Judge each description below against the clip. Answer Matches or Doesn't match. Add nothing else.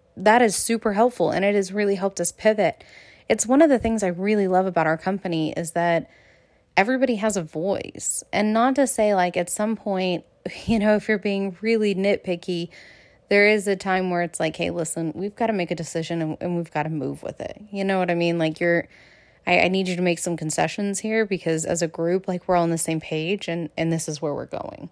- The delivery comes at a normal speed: Doesn't match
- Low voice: Doesn't match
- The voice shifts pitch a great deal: Doesn't match